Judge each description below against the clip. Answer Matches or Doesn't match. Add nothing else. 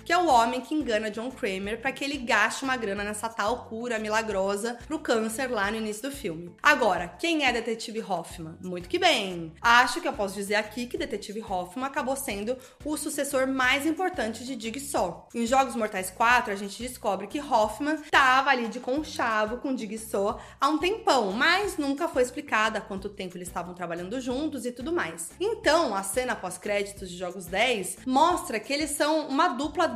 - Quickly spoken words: Matches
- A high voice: Matches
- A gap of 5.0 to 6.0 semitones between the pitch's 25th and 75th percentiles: Matches